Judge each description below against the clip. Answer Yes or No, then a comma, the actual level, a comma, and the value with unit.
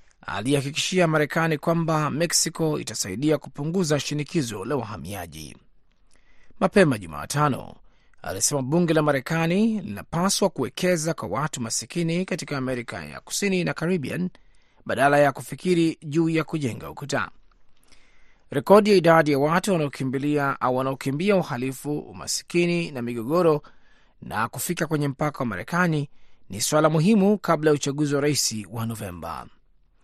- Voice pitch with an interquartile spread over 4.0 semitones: Yes, average, 4.6 semitones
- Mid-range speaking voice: Yes, medium, 150 Hz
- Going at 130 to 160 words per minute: No, average, 120 wpm